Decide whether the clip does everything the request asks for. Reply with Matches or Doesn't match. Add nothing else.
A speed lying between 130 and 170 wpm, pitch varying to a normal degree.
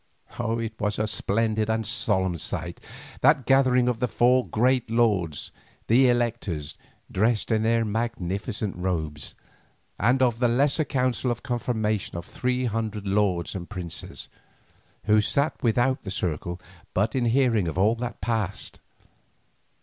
Matches